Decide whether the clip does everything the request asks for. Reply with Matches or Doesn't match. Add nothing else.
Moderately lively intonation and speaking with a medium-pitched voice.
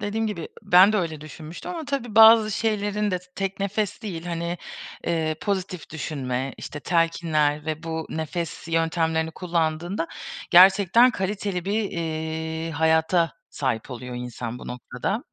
Matches